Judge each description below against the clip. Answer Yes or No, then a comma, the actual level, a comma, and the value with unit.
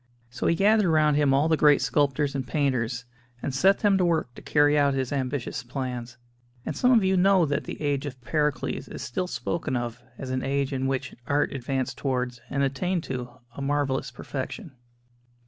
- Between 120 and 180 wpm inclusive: No, average, 195 wpm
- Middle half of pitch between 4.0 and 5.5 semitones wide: No, average, 3.2 semitones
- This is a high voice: No, medium, 140 Hz